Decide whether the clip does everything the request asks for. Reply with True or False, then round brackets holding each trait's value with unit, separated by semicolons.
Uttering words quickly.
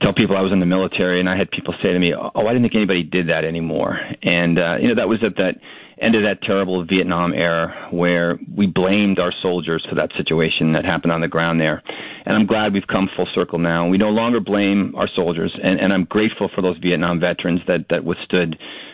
True (240 wpm)